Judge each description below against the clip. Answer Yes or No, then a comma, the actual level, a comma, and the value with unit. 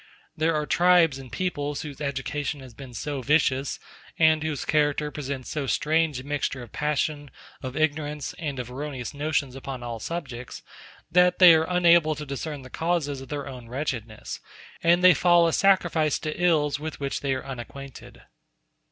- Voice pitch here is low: No, medium, 145 Hz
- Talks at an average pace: Yes, average, 170 wpm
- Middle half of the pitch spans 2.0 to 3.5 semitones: Yes, average, 2.8 semitones